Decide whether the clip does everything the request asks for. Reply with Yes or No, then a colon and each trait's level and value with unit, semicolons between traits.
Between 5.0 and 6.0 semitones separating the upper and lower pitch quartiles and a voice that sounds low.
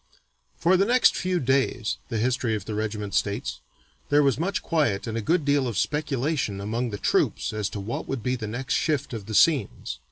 Yes: wide, 5.4 semitones; low, 125 Hz